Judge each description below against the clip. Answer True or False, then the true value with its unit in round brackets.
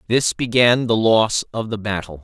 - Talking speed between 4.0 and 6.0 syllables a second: True (4.6 syllables/s)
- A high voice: False (110 Hz)